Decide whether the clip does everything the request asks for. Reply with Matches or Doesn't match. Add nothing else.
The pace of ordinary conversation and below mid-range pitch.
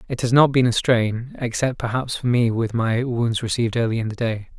Doesn't match